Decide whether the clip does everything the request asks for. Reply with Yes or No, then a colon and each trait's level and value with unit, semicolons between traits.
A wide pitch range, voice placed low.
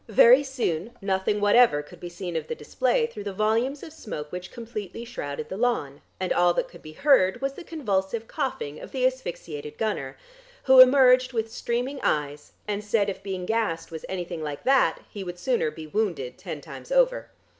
No: wide, 6.5 semitones; high, 210 Hz